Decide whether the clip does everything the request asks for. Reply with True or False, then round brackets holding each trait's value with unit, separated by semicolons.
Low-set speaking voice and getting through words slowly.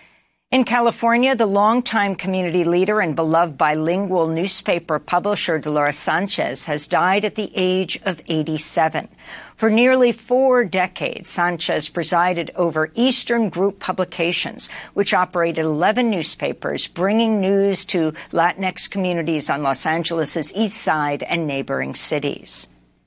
False (180 Hz; 120 wpm)